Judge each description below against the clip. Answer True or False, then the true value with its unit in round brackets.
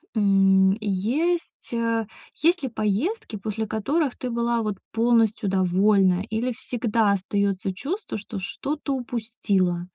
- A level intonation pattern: False (3.8 semitones)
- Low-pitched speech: False (220 Hz)